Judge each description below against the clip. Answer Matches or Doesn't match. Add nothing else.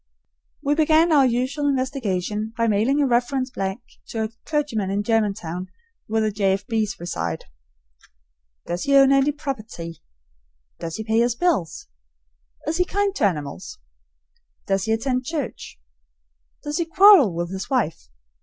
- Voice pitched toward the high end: Matches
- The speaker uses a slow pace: Doesn't match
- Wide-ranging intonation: Matches